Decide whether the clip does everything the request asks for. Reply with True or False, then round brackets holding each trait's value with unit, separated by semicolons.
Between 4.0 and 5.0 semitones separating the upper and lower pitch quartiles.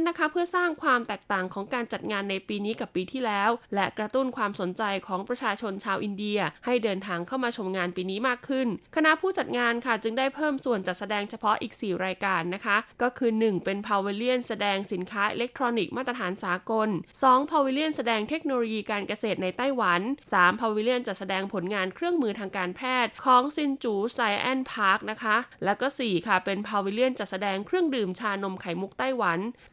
True (4.4 semitones)